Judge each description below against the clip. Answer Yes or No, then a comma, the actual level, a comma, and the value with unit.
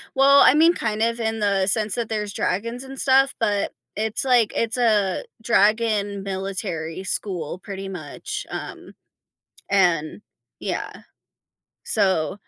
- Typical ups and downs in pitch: Yes, average, 3.2 semitones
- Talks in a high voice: Yes, high, 210 Hz